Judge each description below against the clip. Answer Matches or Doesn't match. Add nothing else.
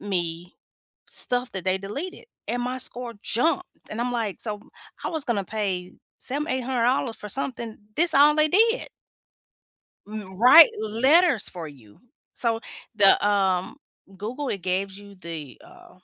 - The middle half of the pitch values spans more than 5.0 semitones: Matches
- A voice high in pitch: Matches